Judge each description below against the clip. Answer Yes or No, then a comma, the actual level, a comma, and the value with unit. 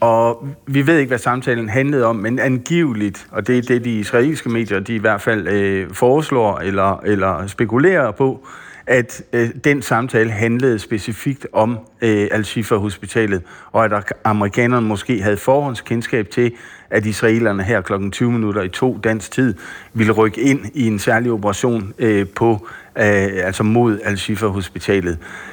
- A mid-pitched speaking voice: No, low, 115 Hz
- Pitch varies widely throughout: No, average, 2.9 semitones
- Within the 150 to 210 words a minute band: Yes, average, 155 wpm